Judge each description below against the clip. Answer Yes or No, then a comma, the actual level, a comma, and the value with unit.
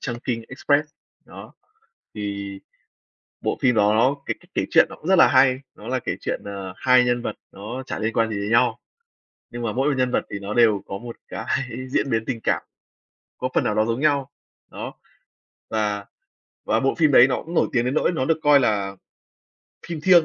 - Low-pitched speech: Yes, low, 120 Hz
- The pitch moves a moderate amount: Yes, average, 3.8 semitones